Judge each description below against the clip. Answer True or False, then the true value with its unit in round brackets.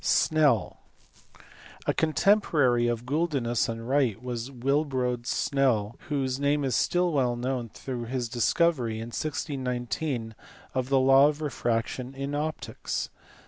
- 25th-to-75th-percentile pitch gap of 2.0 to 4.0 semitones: True (3.4 semitones)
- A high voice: False (130 Hz)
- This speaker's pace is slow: True (125 wpm)